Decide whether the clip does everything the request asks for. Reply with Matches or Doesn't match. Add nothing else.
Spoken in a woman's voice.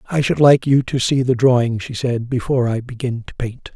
Doesn't match